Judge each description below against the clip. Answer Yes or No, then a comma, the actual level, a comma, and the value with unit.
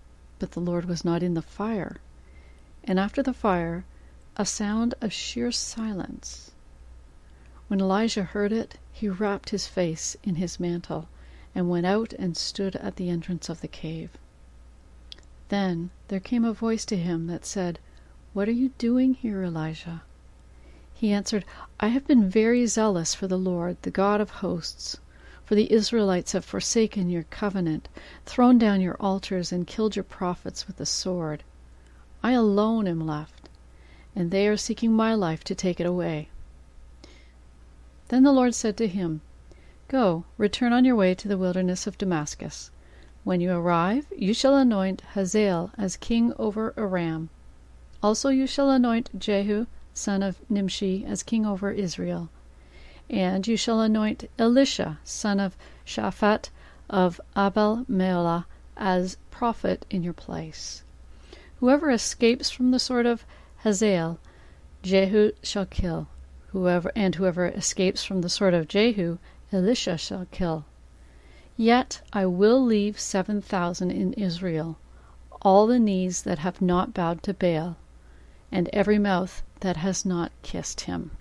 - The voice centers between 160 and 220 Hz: Yes, medium, 185 Hz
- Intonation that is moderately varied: Yes, average, 4.9 semitones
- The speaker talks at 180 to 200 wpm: No, average, 150 wpm